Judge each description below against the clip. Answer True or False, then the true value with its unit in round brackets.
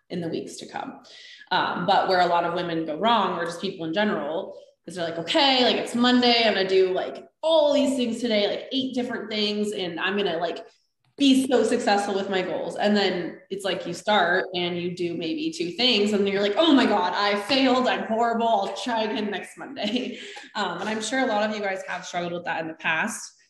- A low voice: False (205 Hz)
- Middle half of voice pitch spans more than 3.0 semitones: True (4.6 semitones)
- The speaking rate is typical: False (235 wpm)